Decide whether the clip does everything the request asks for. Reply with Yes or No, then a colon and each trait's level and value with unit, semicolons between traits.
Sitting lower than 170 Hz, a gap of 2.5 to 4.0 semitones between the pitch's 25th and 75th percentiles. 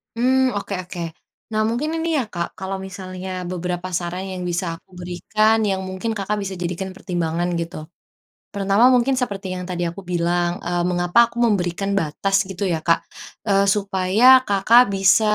No: high, 190 Hz; average, 2.9 semitones